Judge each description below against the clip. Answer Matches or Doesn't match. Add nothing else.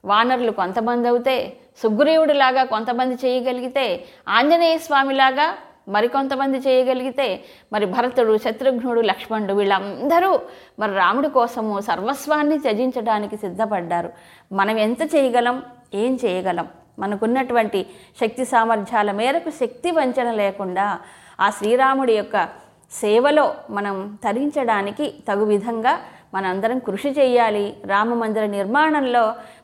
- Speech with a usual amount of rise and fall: Matches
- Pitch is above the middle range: Matches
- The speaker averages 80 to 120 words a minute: Matches